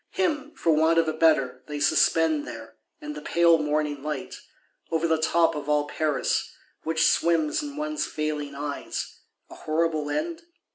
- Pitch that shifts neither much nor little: No, narrow, 2.0 semitones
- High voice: No, medium, 155 Hz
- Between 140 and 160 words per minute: Yes, average, 155 wpm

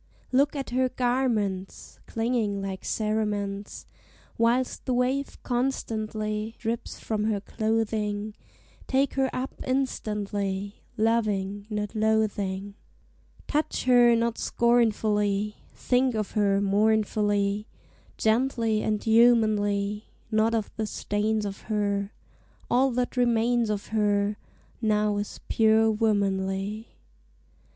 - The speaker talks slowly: Yes, slow, 105 wpm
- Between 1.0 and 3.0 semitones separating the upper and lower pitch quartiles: Yes, narrow, 2.4 semitones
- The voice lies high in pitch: Yes, high, 215 Hz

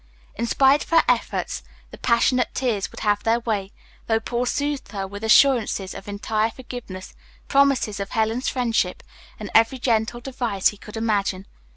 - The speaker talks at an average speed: Yes, average, 165 wpm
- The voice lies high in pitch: Yes, high, 225 Hz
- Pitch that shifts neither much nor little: Yes, average, 3.5 semitones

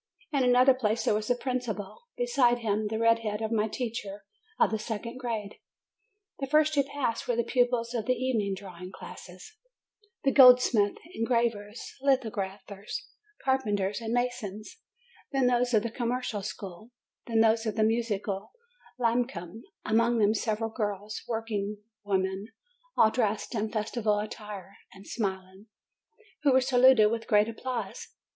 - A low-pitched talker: No, high, 225 Hz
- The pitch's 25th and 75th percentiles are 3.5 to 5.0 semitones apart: No, average, 3.0 semitones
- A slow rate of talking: No, average, 150 wpm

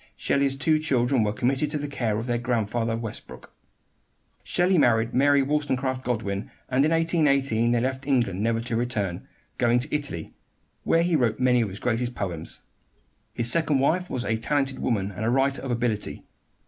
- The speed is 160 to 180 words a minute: Yes, average, 175 wpm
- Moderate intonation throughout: Yes, average, 3.6 semitones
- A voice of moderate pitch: No, low, 125 Hz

